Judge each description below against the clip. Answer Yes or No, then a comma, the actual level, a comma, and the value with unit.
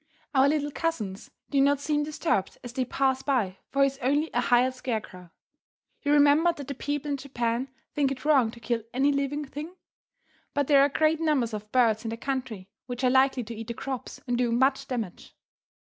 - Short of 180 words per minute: No, fast, 205 wpm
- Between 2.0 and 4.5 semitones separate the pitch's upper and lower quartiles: Yes, average, 3.3 semitones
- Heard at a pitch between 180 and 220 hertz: No, very high, 265 Hz